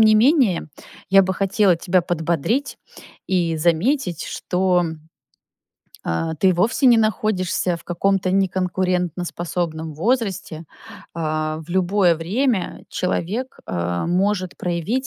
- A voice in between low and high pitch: Yes, medium, 180 Hz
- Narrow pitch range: No, average, 3.3 semitones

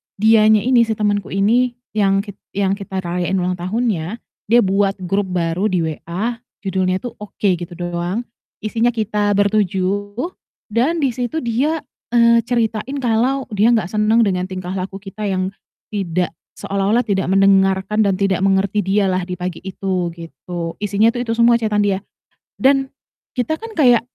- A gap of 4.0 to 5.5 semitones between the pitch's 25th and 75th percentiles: No, average, 3.5 semitones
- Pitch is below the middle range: No, high, 205 Hz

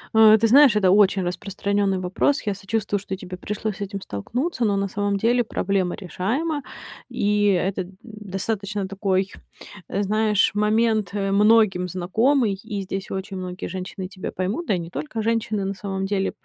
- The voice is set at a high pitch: Yes, high, 200 Hz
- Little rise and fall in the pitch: Yes, narrow, 2.3 semitones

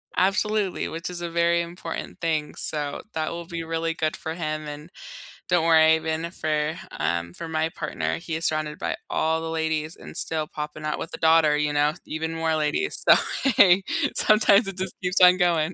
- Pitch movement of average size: No, narrow, 1.8 semitones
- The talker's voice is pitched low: No, medium, 160 Hz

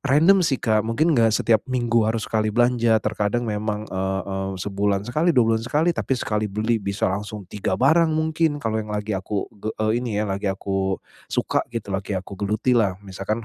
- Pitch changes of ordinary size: Yes, average, 3.2 semitones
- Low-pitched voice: Yes, low, 110 Hz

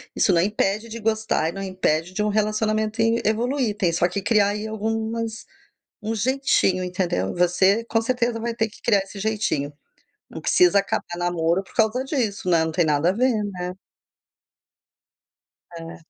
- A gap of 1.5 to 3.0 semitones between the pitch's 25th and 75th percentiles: No, average, 3.8 semitones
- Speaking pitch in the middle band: No, high, 210 Hz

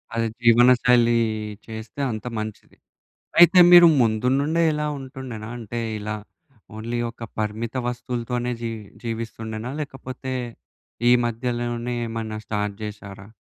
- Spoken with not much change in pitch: Yes, narrow, 2.2 semitones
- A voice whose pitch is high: No, low, 115 Hz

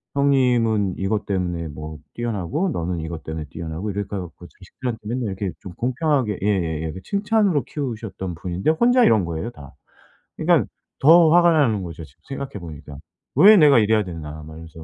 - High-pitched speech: No, low, 100 Hz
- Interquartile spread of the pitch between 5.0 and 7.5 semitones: No, wide, 8.1 semitones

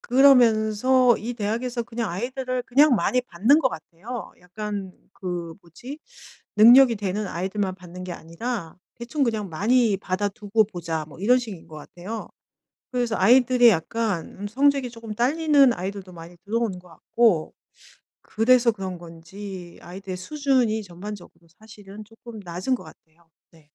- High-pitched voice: Yes, high, 215 Hz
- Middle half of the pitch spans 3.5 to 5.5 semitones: Yes, average, 5.1 semitones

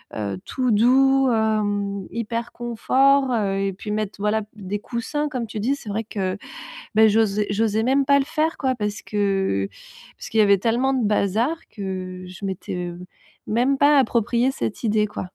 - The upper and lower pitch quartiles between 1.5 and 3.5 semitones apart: No, average, 4.0 semitones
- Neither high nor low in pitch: No, high, 220 Hz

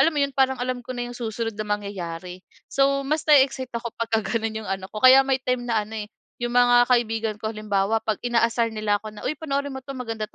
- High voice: Yes, high, 230 Hz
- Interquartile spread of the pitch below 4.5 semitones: Yes, average, 3.2 semitones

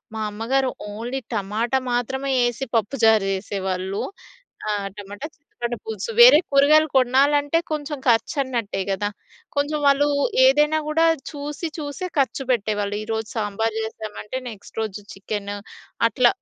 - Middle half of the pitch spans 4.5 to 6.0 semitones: Yes, average, 5.2 semitones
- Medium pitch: No, high, 240 Hz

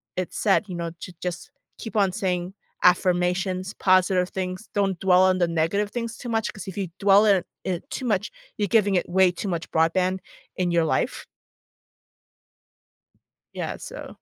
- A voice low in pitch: No, medium, 185 Hz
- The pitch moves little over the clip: Yes, narrow, 2.0 semitones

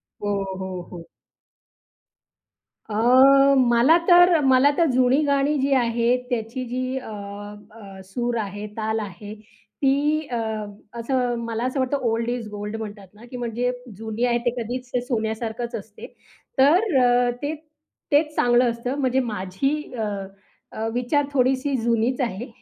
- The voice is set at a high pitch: Yes, high, 245 Hz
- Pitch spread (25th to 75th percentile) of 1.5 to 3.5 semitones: Yes, average, 3.0 semitones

